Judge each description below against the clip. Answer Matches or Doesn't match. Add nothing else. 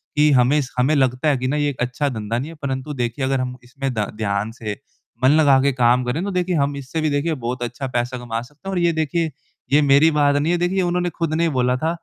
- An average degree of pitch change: Matches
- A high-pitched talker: Doesn't match